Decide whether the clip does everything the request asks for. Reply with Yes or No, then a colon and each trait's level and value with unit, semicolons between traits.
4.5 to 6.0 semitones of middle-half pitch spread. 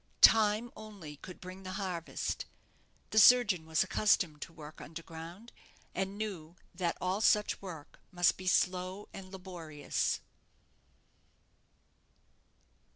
No: average, 3.6 semitones